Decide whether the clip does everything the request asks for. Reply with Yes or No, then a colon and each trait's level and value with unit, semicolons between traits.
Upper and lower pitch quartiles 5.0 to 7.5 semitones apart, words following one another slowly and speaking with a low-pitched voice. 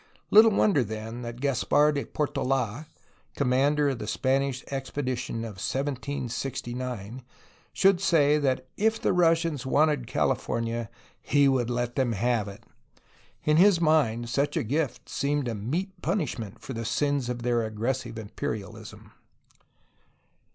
No: average, 3.9 semitones; slow, 130 wpm; low, 130 Hz